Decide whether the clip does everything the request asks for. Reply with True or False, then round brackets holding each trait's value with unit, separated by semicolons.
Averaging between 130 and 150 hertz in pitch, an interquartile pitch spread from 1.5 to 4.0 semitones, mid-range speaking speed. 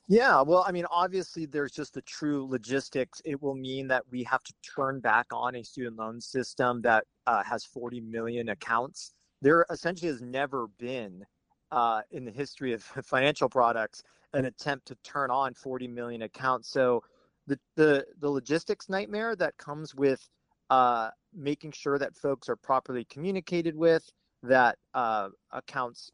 True (135 Hz; 3.5 semitones; 165 wpm)